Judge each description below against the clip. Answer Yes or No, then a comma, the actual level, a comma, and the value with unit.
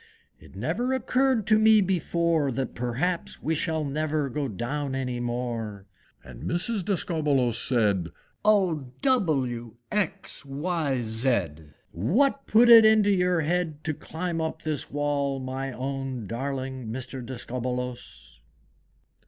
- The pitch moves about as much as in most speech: No, wide, 6.1 semitones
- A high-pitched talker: No, medium, 140 Hz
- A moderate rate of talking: No, slow, 125 wpm